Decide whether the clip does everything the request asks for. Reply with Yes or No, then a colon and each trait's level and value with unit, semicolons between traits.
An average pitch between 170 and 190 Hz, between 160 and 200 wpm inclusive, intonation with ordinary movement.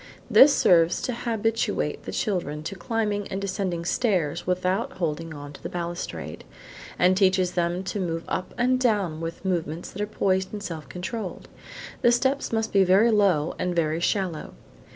Yes: medium, 185 Hz; average, 170 wpm; average, 3.7 semitones